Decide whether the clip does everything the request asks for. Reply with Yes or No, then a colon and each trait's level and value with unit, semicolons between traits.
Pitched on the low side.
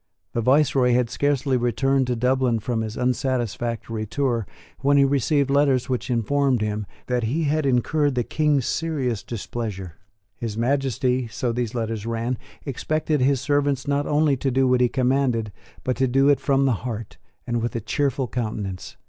Yes: low, 125 Hz